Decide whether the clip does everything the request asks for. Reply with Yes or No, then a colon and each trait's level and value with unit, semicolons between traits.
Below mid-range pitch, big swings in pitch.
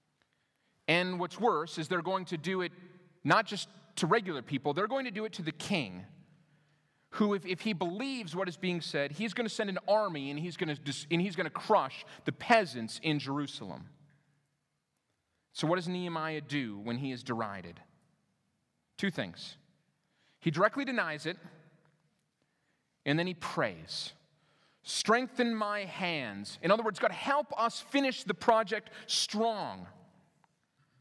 No: medium, 175 Hz; wide, 5.8 semitones